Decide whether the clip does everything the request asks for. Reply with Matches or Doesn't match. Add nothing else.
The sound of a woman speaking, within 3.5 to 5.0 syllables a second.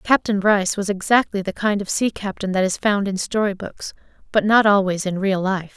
Doesn't match